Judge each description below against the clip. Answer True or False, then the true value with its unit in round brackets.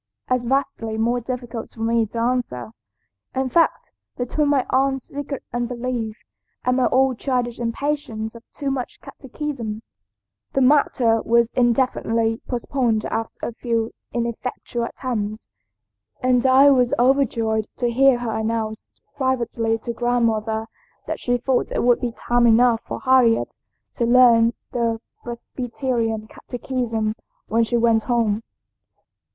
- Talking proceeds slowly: True (130 wpm)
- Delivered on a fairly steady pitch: True (2.1 semitones)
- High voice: True (240 Hz)